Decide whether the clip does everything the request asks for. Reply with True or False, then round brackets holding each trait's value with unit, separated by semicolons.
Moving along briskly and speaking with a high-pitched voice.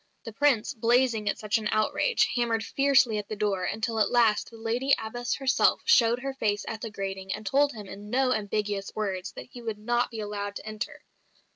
True (210 wpm; 220 Hz)